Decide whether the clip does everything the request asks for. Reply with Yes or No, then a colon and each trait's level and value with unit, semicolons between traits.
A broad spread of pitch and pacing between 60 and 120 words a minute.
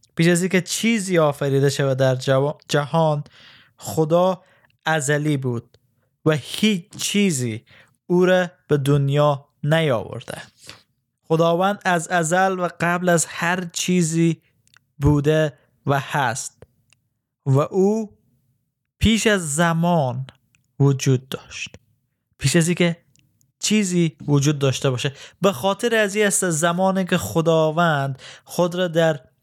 No: average, 4.4 semitones; average, 110 wpm